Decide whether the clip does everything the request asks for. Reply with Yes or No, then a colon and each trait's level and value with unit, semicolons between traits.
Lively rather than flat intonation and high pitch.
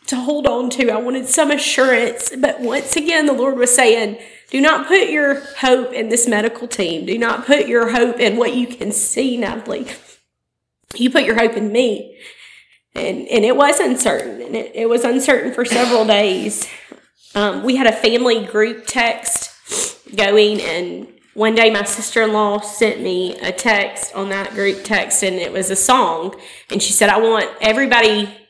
No: average, 3.2 semitones; high, 230 Hz